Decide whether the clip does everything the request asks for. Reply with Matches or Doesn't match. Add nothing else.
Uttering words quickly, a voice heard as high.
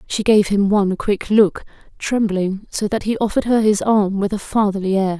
Matches